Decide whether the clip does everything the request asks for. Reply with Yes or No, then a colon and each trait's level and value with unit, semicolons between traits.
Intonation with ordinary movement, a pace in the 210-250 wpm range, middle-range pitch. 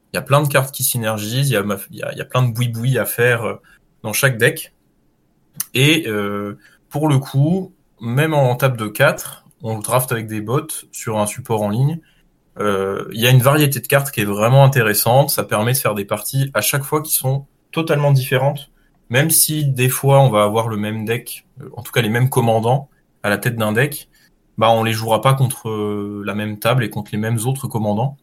No: average, 4.4 semitones; fast, 220 wpm; low, 125 Hz